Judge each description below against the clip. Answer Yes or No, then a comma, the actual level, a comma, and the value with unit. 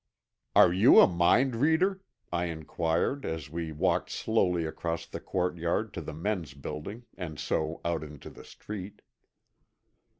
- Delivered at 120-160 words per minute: Yes, average, 140 wpm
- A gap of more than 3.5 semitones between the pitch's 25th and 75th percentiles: Yes, average, 4.5 semitones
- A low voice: Yes, very low, 85 Hz